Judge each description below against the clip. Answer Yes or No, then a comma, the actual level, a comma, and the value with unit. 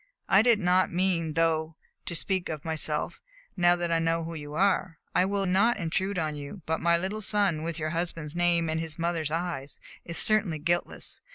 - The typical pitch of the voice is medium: Yes, medium, 170 Hz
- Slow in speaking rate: No, average, 195 wpm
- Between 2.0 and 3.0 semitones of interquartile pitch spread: Yes, narrow, 2.6 semitones